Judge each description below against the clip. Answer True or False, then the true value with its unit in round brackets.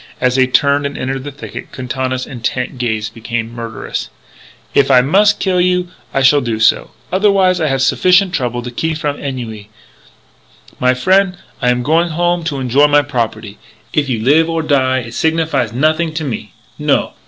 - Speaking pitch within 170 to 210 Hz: False (135 Hz)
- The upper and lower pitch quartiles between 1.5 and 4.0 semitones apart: False (4.7 semitones)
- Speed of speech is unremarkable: True (180 wpm)